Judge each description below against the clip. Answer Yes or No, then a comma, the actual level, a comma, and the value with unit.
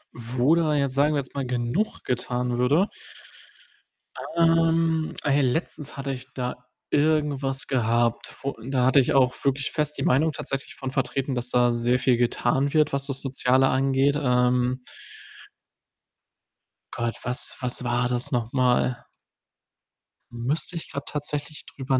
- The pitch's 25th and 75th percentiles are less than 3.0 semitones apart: Yes, narrow, 2.5 semitones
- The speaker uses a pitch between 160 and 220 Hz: No, low, 135 Hz